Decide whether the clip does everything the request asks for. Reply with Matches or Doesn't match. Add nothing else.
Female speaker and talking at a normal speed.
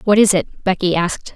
Doesn't match